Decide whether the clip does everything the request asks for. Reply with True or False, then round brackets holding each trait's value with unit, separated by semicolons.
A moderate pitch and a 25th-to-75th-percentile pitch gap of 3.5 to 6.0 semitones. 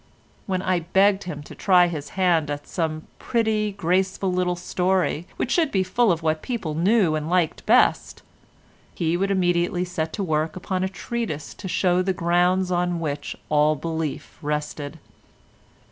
False (180 Hz; 3.0 semitones)